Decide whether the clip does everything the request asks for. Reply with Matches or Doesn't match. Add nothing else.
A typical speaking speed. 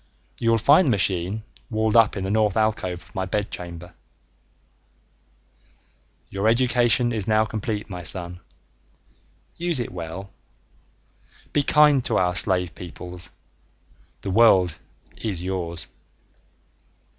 Doesn't match